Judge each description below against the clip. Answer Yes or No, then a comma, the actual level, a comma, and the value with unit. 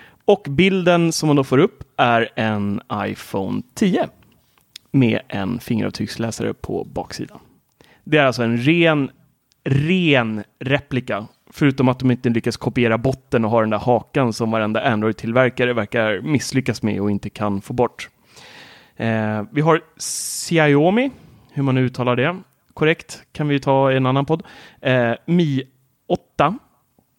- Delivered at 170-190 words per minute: No, average, 140 wpm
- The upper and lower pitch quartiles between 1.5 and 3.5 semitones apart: No, average, 3.9 semitones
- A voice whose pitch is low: Yes, low, 130 Hz